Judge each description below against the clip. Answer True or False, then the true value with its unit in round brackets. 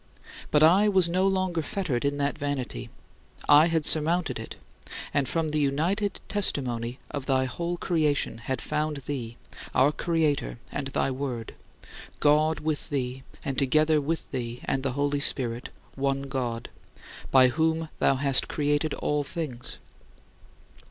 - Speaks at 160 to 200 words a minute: False (145 wpm)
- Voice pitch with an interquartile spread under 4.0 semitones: True (3.3 semitones)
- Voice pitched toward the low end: False (145 Hz)